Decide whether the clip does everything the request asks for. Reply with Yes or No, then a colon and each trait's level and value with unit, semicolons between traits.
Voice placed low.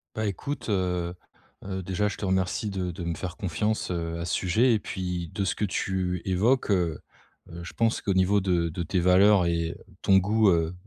Yes: very low, 95 Hz